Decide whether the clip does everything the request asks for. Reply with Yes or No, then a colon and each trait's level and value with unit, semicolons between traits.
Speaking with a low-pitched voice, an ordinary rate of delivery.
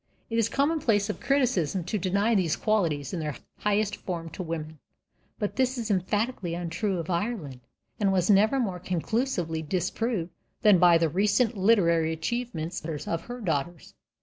No: high, 190 Hz; average, 160 wpm